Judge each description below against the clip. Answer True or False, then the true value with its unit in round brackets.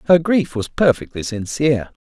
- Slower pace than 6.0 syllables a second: True (5.1 syllables/s)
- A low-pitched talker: True (130 Hz)